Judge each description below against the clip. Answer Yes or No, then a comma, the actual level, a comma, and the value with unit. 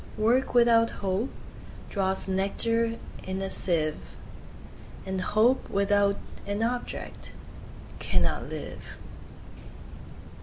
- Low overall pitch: No, high, 205 Hz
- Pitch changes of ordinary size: Yes, average, 3.2 semitones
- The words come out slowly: Yes, slow, 85 wpm